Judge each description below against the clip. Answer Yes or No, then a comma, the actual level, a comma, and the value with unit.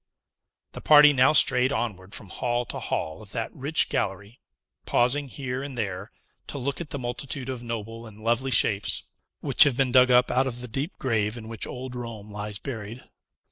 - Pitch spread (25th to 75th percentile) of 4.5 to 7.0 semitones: No, average, 3.4 semitones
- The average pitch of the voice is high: No, low, 120 Hz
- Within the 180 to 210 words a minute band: Yes, average, 190 wpm